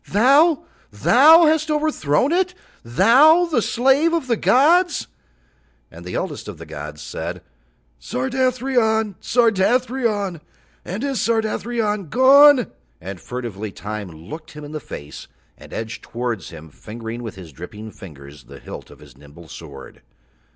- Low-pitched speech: No, high, 200 Hz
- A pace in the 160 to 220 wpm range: No, slow, 135 wpm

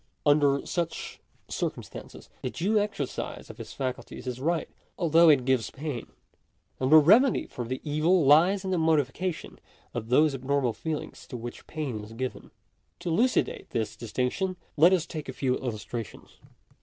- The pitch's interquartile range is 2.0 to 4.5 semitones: No, average, 4.9 semitones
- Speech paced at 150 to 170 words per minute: Yes, average, 155 wpm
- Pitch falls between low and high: Yes, medium, 145 Hz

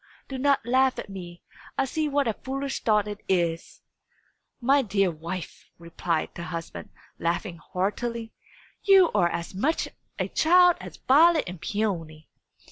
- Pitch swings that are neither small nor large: No, wide, 7.8 semitones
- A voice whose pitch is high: Yes, high, 210 Hz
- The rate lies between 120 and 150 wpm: Yes, average, 145 wpm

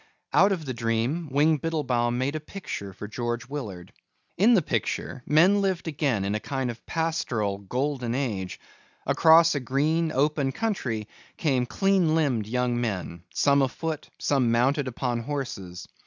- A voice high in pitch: No, low, 135 Hz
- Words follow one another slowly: No, average, 155 wpm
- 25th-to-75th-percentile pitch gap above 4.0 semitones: Yes, average, 5.0 semitones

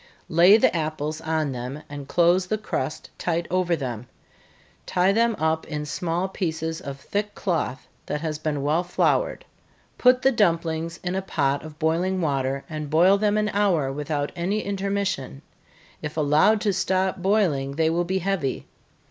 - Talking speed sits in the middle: Yes, average, 165 wpm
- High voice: No, medium, 165 Hz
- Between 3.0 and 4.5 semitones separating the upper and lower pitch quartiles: Yes, average, 4.2 semitones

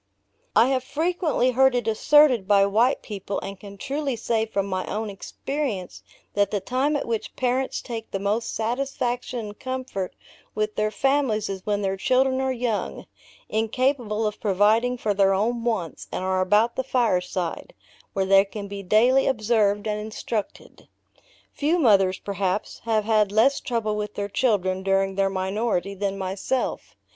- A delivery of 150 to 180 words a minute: Yes, average, 160 wpm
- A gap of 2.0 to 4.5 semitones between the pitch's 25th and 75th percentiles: Yes, average, 4.1 semitones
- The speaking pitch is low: No, high, 215 Hz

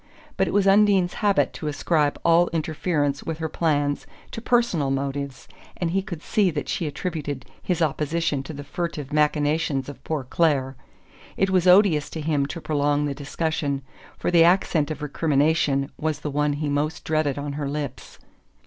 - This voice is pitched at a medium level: Yes, medium, 150 Hz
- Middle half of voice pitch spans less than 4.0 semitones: Yes, average, 2.7 semitones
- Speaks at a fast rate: No, average, 175 wpm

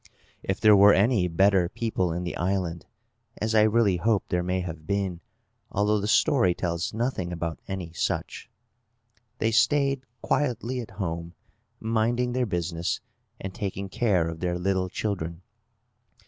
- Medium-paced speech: Yes, average, 150 wpm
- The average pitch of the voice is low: Yes, very low, 95 Hz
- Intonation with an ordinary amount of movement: Yes, average, 4.0 semitones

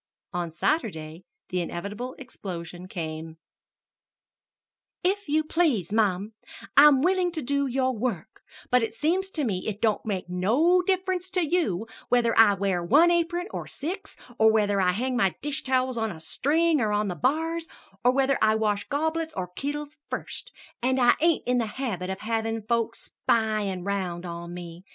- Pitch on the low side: No, high, 230 Hz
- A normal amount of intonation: No, wide, 7.7 semitones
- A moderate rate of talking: Yes, average, 165 wpm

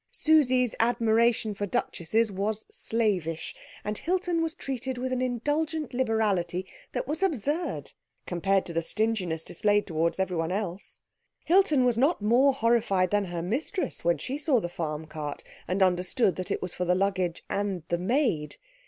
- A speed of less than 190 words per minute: Yes, average, 160 wpm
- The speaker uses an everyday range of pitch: No, wide, 6.1 semitones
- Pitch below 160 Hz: No, high, 215 Hz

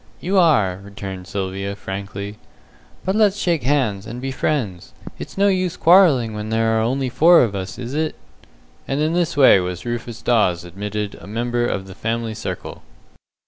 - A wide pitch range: Yes, wide, 6.7 semitones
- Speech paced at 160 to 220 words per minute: Yes, average, 175 wpm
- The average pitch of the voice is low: Yes, low, 115 Hz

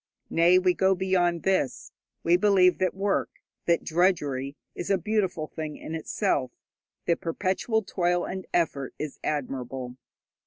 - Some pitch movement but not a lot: Yes, average, 3.6 semitones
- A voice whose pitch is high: No, medium, 175 Hz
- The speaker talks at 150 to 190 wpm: No, average, 140 wpm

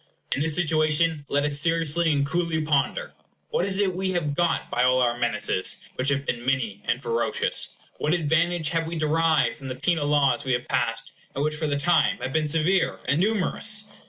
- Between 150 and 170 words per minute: No, average, 200 wpm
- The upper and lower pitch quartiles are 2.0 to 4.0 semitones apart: Yes, average, 3.6 semitones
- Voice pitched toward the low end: No, medium, 155 Hz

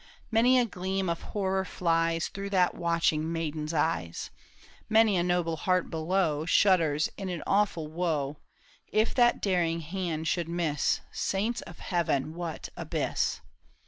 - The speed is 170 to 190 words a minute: No, average, 145 wpm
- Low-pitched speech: No, medium, 175 Hz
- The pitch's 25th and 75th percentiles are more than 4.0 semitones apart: No, average, 3.0 semitones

